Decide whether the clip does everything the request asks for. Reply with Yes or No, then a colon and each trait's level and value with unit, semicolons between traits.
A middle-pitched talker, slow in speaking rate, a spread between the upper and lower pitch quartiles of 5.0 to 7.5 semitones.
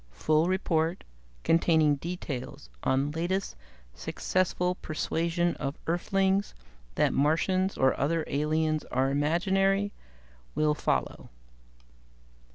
No: medium, 165 Hz; slow, 90 wpm; average, 3.9 semitones